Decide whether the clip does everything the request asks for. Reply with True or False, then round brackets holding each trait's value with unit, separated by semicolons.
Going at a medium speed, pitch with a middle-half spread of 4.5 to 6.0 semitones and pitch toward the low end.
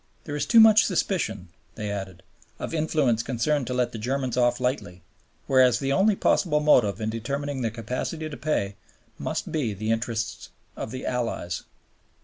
True (165 wpm; 5.0 semitones; 125 Hz)